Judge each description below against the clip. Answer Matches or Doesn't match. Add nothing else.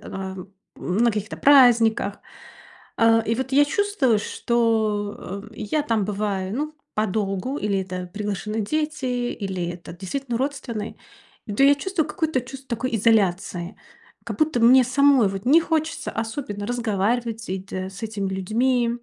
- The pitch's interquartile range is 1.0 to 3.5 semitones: Doesn't match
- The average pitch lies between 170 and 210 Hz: Doesn't match